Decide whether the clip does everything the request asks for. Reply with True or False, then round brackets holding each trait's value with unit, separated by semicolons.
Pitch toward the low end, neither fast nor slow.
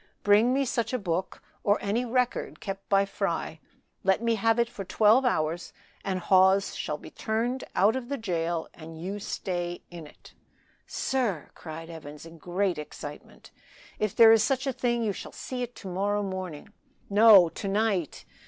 False (200 Hz; 175 wpm)